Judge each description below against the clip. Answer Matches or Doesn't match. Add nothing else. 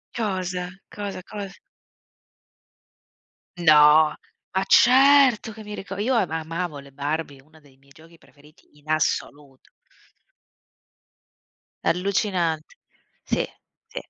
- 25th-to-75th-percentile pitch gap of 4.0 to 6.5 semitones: Matches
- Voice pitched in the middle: Matches